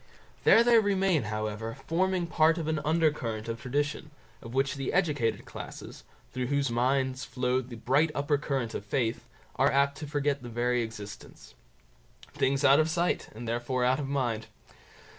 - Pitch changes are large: No, average, 4.3 semitones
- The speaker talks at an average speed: Yes, average, 170 wpm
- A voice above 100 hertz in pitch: Yes, low, 135 Hz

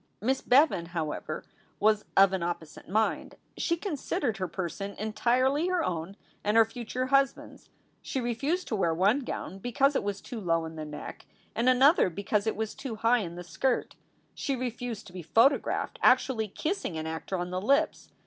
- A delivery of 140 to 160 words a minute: No, average, 185 wpm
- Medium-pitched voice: No, high, 220 Hz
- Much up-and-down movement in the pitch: Yes, wide, 6.1 semitones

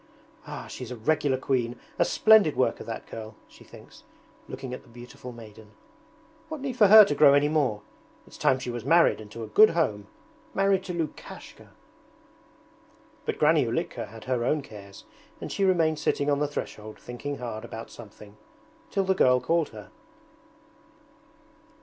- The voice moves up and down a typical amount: No, wide, 6.4 semitones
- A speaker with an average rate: Yes, average, 170 wpm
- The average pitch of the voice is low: Yes, low, 130 Hz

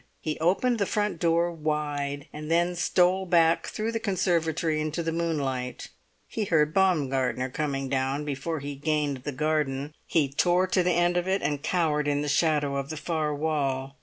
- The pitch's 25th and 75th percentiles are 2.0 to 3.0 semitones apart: No, average, 3.4 semitones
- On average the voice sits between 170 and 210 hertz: No, medium, 155 Hz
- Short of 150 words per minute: No, average, 180 wpm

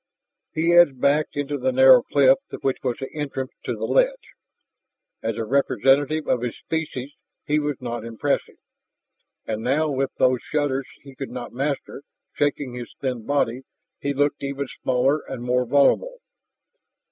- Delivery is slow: No, average, 155 wpm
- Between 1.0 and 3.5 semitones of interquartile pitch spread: Yes, narrow, 2.4 semitones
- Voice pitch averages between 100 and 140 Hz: Yes, low, 135 Hz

